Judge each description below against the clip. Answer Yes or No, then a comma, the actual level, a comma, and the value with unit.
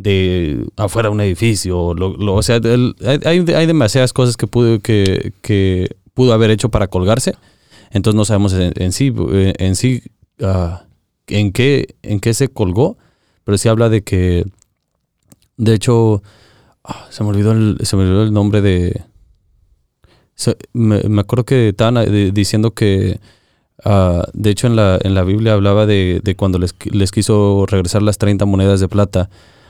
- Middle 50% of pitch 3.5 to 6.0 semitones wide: No, average, 2.8 semitones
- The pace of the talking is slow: No, average, 170 wpm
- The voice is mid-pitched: No, low, 105 Hz